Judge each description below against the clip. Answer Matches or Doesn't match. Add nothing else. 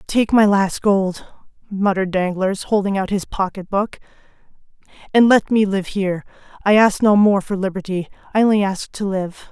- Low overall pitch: Doesn't match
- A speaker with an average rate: Matches